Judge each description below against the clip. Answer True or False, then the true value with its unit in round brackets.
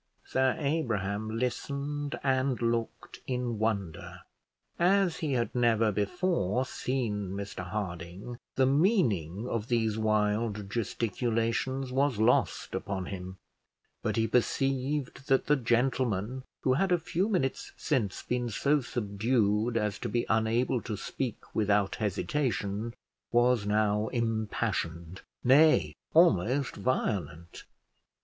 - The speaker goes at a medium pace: False (115 wpm)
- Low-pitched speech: True (115 Hz)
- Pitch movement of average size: True (4.2 semitones)